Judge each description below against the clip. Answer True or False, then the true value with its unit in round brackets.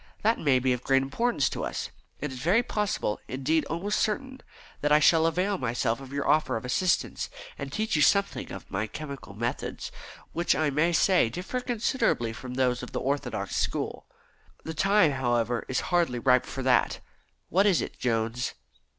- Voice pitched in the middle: True (145 Hz)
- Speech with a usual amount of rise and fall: False (6.4 semitones)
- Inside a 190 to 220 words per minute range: False (180 wpm)